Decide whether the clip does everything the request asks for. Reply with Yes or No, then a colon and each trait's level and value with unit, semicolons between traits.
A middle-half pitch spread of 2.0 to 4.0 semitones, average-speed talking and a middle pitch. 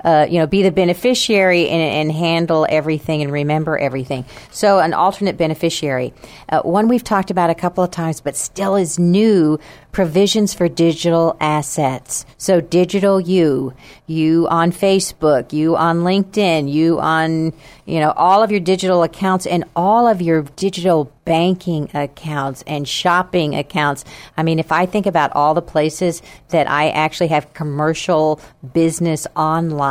Yes: average, 3.1 semitones; average, 155 wpm; medium, 165 Hz